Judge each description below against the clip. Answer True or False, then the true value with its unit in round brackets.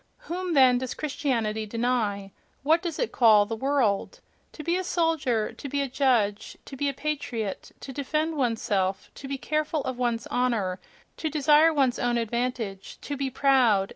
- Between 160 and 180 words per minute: True (175 wpm)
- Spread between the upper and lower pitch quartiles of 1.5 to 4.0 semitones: False (4.7 semitones)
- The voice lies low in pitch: False (260 Hz)